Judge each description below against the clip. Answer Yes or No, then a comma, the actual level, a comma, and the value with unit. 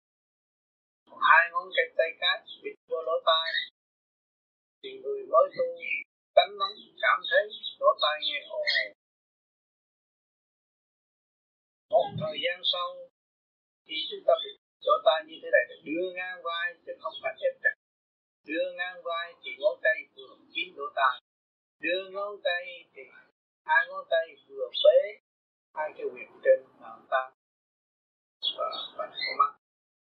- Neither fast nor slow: No, slow, 145 wpm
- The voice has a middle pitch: No, very high, 305 Hz